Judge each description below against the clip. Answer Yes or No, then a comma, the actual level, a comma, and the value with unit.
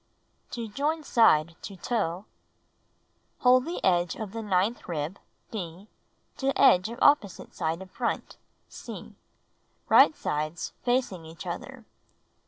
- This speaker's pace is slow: Yes, slow, 125 wpm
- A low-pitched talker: No, high, 200 Hz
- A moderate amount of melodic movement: No, wide, 6.1 semitones